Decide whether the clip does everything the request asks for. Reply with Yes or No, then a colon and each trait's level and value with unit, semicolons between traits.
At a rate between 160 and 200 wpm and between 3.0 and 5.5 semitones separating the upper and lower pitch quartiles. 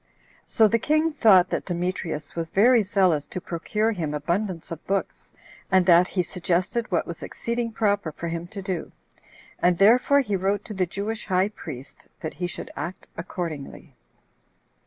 Yes: average, 165 wpm; average, 3.8 semitones